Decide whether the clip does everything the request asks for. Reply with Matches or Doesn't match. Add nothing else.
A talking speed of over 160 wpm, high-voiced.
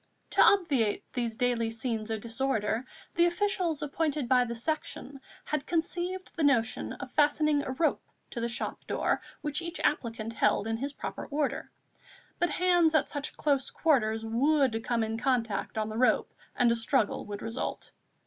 Matches